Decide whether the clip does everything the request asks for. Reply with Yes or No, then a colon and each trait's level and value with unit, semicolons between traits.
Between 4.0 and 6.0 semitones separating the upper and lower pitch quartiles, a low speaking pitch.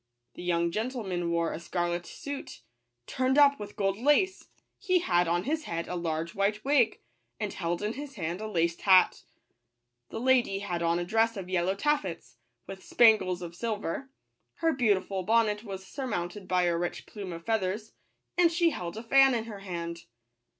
No: average, 5.2 semitones; high, 195 Hz